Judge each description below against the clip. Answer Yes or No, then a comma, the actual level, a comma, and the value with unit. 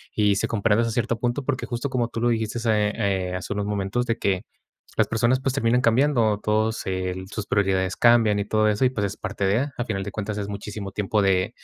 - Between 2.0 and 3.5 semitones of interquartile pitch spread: Yes, average, 2.9 semitones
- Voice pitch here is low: Yes, low, 105 Hz